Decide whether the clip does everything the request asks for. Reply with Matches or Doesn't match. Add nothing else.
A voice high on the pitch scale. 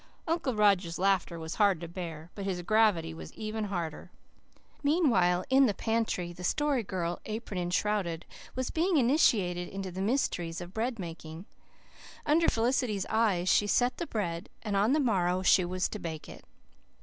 Matches